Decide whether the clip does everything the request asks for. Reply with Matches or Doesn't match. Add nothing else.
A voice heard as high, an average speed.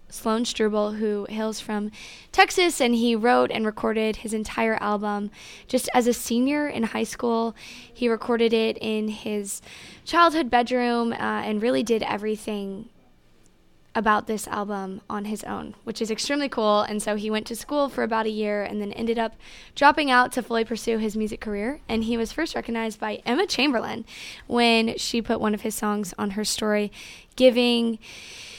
Matches